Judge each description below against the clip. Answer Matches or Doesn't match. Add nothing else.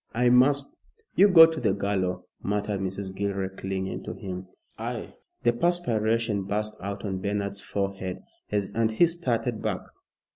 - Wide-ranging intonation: Doesn't match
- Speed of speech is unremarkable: Matches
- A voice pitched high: Doesn't match